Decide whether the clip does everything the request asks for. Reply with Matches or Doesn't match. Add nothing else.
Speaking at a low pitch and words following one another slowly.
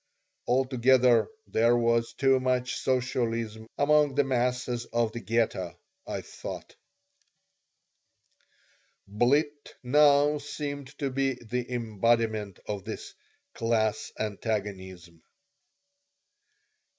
Matches